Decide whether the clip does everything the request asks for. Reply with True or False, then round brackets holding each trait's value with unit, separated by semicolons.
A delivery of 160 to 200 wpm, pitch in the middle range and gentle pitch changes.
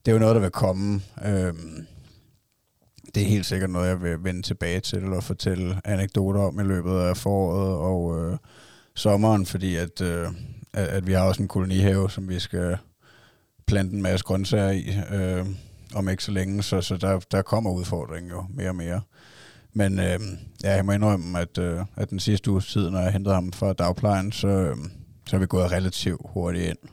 False (195 wpm; 95 Hz; 1.9 semitones)